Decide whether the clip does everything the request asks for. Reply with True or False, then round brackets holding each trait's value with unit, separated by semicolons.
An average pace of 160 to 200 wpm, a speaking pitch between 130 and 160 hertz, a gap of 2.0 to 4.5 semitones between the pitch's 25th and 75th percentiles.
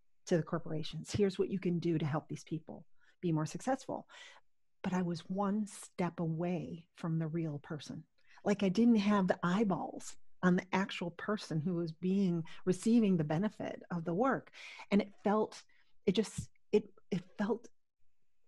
False (170 wpm; 185 Hz; 3.5 semitones)